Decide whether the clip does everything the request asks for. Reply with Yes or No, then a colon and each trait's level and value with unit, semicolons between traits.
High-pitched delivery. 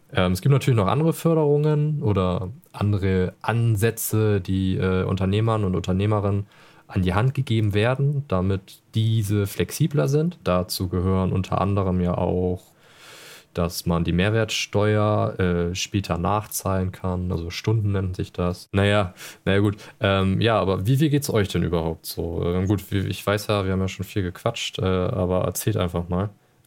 No: low, 100 Hz